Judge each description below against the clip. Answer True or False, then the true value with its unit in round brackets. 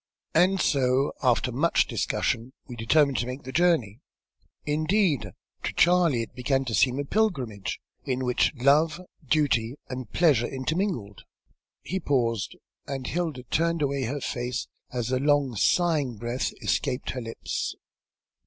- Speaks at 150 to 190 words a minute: False (140 wpm)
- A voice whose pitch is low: True (130 Hz)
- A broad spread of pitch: False (4.2 semitones)